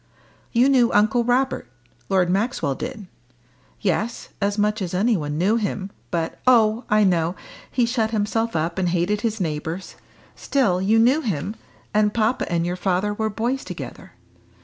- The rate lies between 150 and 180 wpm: Yes, average, 160 wpm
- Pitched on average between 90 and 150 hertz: No, high, 210 Hz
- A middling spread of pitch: Yes, average, 4.2 semitones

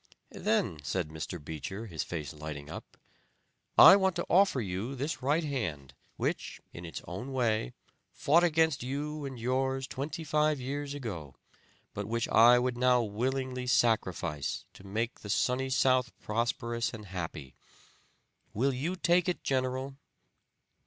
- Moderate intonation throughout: No, wide, 5.9 semitones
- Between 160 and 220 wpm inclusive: No, average, 140 wpm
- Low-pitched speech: Yes, low, 125 Hz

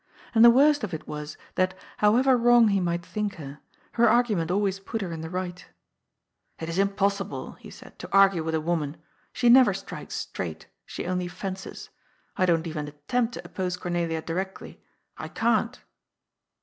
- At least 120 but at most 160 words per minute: No, average, 180 wpm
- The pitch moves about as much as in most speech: Yes, average, 4.9 semitones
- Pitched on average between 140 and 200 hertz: Yes, high, 190 Hz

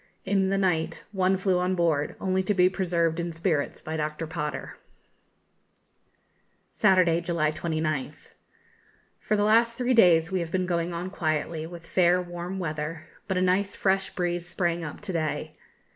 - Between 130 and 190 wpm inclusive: Yes, average, 160 wpm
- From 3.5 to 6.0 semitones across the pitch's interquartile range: No, narrow, 2.5 semitones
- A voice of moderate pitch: Yes, medium, 175 Hz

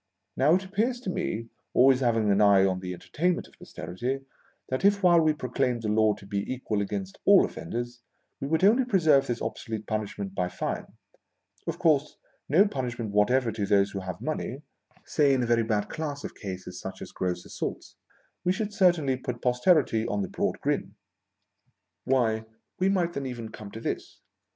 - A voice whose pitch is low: Yes, low, 120 Hz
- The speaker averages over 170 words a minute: Yes, average, 190 wpm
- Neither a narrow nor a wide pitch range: No, wide, 6.9 semitones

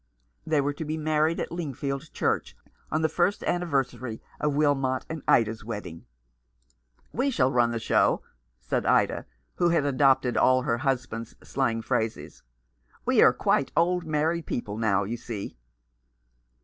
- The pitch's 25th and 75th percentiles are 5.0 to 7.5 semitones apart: Yes, wide, 5.4 semitones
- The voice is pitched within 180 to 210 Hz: No, low, 135 Hz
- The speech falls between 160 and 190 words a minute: No, average, 150 wpm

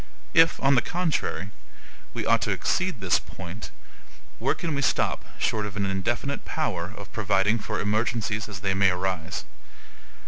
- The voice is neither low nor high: No, low, 105 Hz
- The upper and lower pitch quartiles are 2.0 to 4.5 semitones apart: No, average, 5.2 semitones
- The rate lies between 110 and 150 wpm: No, average, 160 wpm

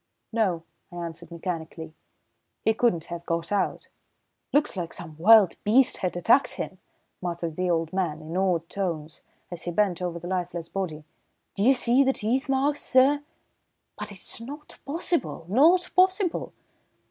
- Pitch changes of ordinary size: No, wide, 7.3 semitones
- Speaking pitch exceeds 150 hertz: Yes, medium, 185 Hz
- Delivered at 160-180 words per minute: No, average, 150 wpm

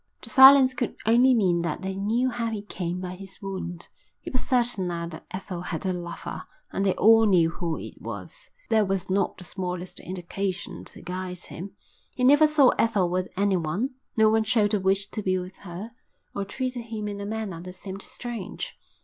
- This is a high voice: Yes, high, 195 Hz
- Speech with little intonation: No, average, 3.7 semitones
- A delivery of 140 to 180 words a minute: No, average, 200 wpm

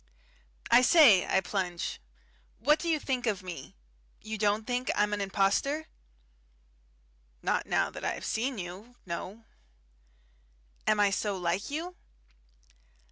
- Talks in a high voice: Yes, high, 210 Hz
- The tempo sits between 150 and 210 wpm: No, slow, 135 wpm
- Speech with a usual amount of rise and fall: Yes, average, 4.6 semitones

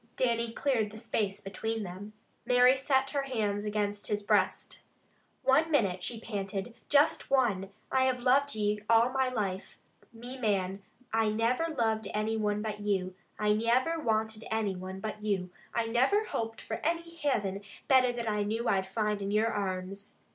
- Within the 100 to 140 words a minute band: No, average, 170 wpm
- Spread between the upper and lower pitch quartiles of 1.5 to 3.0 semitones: No, average, 3.5 semitones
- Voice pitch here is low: No, high, 220 Hz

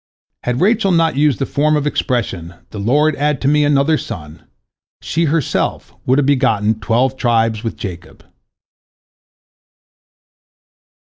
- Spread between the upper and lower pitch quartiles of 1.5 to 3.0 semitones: No, average, 4.9 semitones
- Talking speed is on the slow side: Yes, slow, 130 wpm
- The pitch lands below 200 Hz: Yes, low, 135 Hz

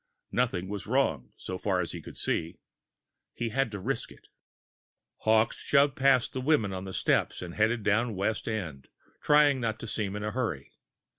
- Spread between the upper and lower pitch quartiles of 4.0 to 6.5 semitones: Yes, average, 5.0 semitones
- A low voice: Yes, low, 110 Hz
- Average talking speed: Yes, average, 180 wpm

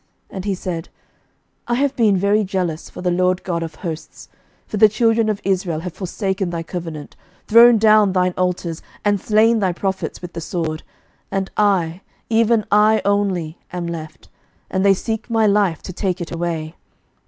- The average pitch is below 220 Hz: Yes, high, 190 Hz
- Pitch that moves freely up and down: No, average, 3.5 semitones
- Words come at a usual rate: Yes, average, 175 wpm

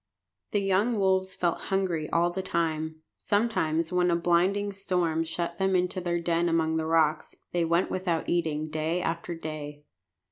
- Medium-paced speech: Yes, average, 165 wpm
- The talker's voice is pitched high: No, medium, 170 Hz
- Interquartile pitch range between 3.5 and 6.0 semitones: No, narrow, 2.6 semitones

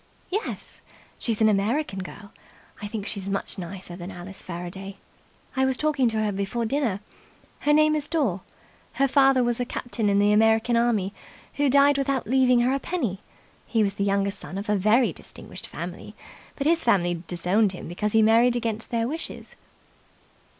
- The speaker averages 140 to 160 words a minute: No, average, 180 wpm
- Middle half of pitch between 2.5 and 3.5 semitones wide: No, average, 4.9 semitones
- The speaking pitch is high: Yes, high, 220 Hz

